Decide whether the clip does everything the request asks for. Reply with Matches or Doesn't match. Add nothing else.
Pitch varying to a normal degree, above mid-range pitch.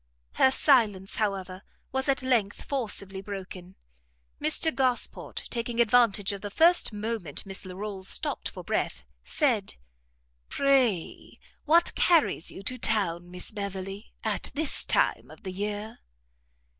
Matches